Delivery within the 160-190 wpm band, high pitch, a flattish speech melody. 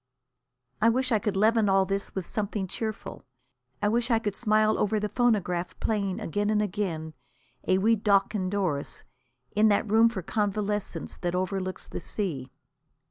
Yes: average, 165 wpm; high, 205 Hz; narrow, 2.3 semitones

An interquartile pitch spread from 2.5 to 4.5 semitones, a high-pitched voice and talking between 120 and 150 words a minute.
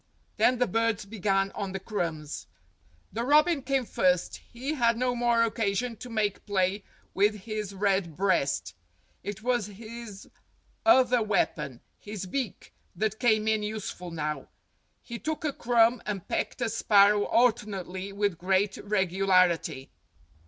Yes: average, 3.6 semitones; high, 210 Hz; average, 140 wpm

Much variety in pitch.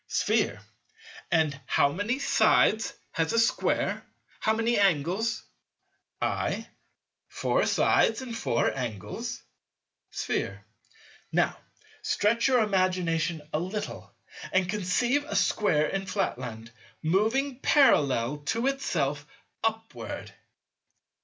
Yes: wide, 7.2 semitones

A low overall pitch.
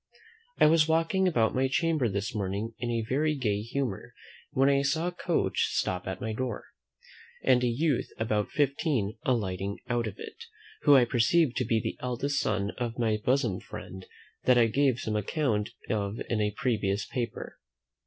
Yes: low, 120 Hz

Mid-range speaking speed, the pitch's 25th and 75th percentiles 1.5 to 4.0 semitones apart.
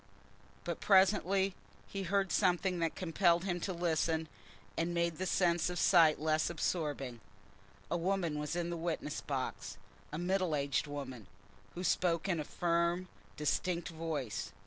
Yes: average, 145 wpm; average, 2.8 semitones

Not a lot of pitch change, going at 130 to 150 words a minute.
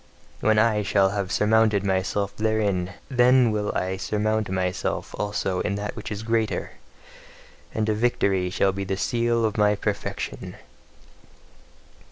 Yes: narrow, 2.1 semitones; average, 140 wpm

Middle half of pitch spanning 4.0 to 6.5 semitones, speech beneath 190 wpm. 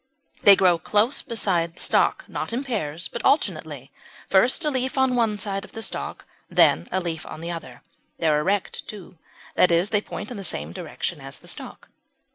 No: wide, 5.4 semitones; average, 200 wpm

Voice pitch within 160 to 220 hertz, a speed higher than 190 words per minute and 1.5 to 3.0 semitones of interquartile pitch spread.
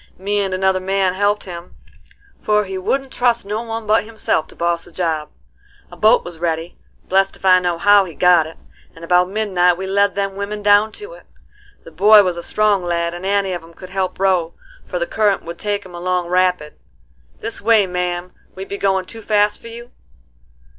Yes: high, 190 Hz; average, 200 wpm; average, 2.7 semitones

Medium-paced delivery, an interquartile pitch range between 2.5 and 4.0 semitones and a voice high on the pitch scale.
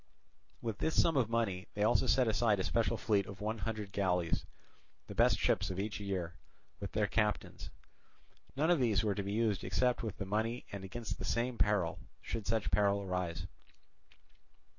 No: average, 185 wpm; average, 2.8 semitones; low, 105 Hz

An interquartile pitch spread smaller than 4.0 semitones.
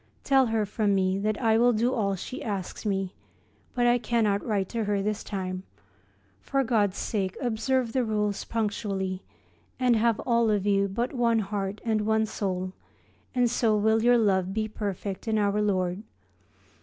Yes: average, 2.7 semitones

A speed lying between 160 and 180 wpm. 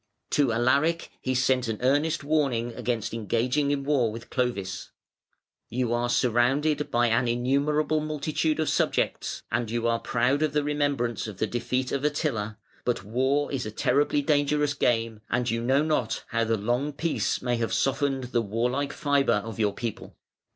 Yes: average, 170 wpm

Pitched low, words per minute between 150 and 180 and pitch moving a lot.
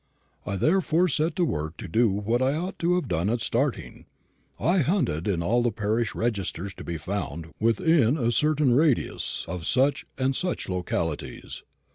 Yes: low, 120 Hz; average, 170 wpm; wide, 8.1 semitones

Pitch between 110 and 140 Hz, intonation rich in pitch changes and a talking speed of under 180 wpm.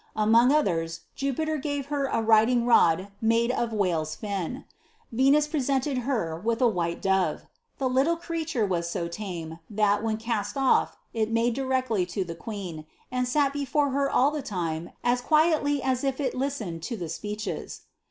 No: high, 230 Hz; wide, 6.0 semitones; average, 170 wpm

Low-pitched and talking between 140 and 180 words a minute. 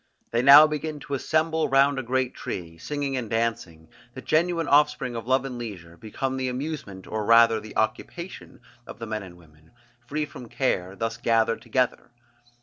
Yes: low, 125 Hz; average, 175 wpm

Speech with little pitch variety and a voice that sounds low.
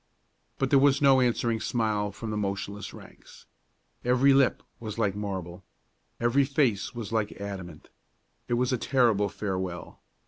No: average, 4.0 semitones; low, 110 Hz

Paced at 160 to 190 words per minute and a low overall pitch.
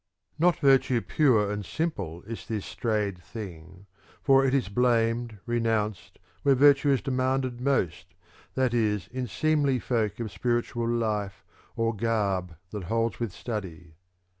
No: average, 140 wpm; low, 115 Hz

